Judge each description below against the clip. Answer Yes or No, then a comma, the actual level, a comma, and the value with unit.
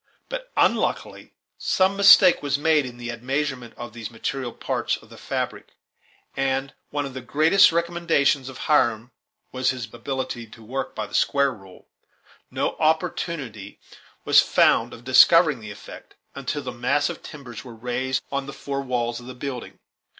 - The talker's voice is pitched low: Yes, low, 130 Hz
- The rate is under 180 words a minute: Yes, average, 165 wpm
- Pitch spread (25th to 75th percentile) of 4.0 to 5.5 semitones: No, average, 3.4 semitones